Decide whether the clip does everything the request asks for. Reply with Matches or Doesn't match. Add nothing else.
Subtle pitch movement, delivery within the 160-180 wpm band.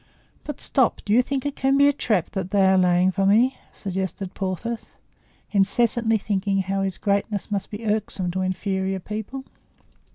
Doesn't match